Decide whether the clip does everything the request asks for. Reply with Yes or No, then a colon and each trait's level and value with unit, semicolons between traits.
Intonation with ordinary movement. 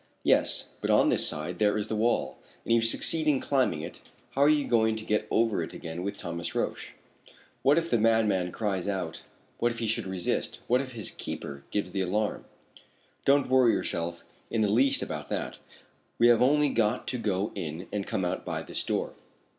Yes: average, 4.6 semitones